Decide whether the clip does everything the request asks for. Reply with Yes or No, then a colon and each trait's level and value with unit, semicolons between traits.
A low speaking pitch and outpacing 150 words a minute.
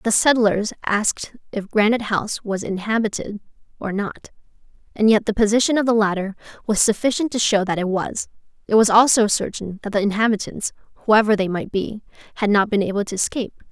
No: high, 210 Hz; average, 180 wpm